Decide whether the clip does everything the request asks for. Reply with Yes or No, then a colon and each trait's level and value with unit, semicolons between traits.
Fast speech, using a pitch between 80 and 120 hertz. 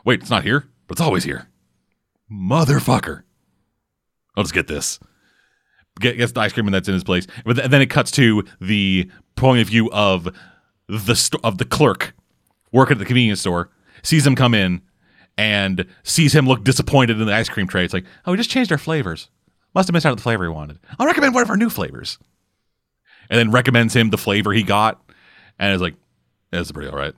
Yes: fast, 215 wpm; low, 110 Hz